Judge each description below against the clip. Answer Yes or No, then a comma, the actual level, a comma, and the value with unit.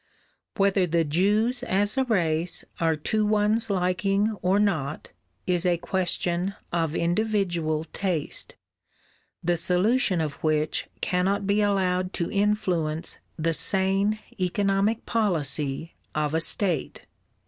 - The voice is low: No, medium, 185 Hz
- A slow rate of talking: Yes, slow, 115 wpm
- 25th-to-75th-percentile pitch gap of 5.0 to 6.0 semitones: No, average, 3.7 semitones